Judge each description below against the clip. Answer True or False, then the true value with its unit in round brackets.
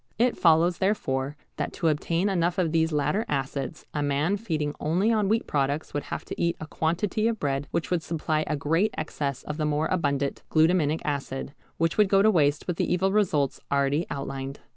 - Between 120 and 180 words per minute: False (200 wpm)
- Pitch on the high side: False (160 Hz)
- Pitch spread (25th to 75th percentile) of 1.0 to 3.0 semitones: False (4.0 semitones)